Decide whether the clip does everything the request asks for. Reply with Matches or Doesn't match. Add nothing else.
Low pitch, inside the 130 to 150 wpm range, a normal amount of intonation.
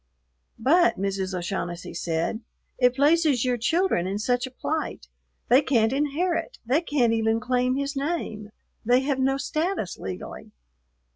Doesn't match